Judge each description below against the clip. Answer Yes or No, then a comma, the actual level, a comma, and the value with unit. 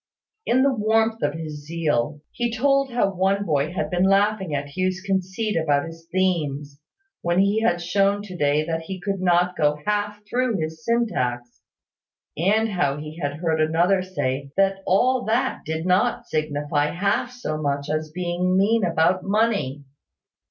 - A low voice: No, medium, 180 Hz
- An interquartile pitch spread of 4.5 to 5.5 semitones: Yes, average, 4.9 semitones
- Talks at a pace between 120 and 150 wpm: No, average, 165 wpm